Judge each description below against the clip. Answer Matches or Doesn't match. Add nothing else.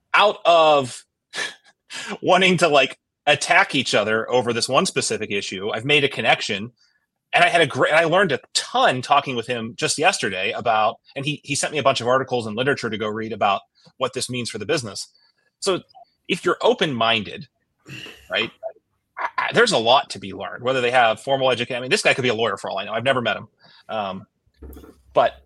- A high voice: Doesn't match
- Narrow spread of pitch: Doesn't match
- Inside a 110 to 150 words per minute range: Doesn't match